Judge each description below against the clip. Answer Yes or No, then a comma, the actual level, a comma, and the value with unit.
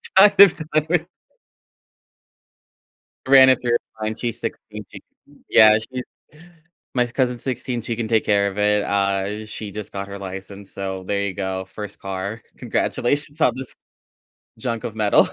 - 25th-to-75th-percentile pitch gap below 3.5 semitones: No, average, 3.9 semitones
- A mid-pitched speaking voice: No, low, 110 Hz